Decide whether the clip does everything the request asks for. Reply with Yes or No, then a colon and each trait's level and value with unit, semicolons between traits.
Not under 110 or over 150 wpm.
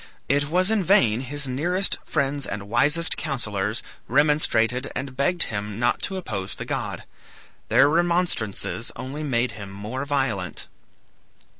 Yes: slow, 135 wpm